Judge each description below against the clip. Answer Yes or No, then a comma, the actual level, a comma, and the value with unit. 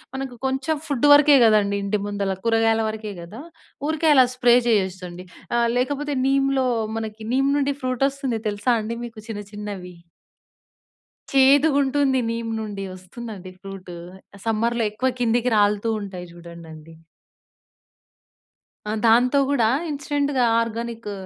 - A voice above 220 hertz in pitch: Yes, high, 230 Hz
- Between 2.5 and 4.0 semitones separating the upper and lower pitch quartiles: No, average, 4.7 semitones